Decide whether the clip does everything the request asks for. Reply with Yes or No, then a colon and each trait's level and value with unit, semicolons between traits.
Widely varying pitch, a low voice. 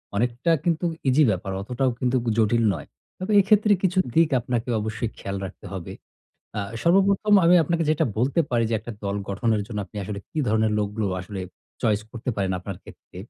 Yes: wide, 7.5 semitones; low, 115 Hz